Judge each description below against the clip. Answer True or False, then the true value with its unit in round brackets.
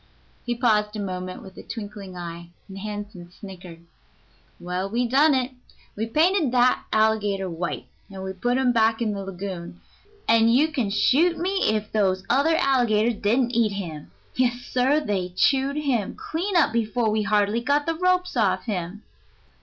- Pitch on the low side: False (220 Hz)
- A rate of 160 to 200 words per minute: True (165 wpm)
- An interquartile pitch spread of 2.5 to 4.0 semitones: False (4.8 semitones)